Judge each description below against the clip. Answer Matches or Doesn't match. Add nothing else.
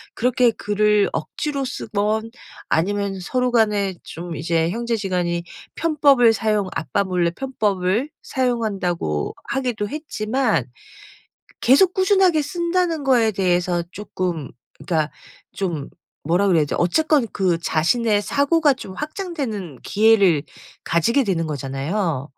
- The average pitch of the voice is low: Doesn't match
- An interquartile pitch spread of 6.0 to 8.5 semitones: Matches